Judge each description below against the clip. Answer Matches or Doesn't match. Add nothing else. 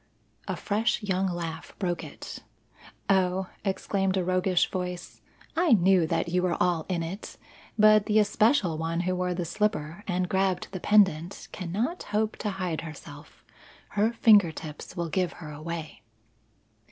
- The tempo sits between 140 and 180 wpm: Matches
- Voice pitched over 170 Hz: Matches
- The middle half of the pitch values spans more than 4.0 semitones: Doesn't match